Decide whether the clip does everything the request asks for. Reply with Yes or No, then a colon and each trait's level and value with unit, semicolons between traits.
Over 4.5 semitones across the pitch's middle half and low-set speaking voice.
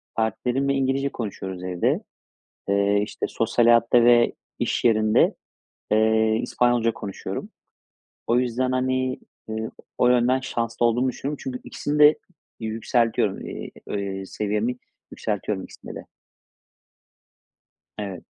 No: average, 2.9 semitones; low, 115 Hz